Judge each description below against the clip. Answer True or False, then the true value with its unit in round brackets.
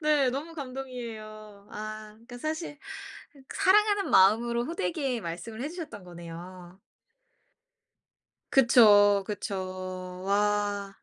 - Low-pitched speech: False (215 Hz)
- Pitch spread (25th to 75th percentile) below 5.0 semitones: False (5.4 semitones)